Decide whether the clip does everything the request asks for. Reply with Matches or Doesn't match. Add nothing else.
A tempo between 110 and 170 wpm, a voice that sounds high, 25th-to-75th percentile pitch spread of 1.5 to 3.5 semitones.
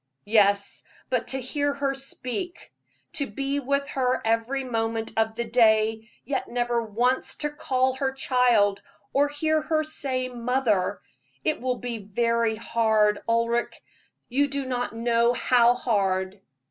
Matches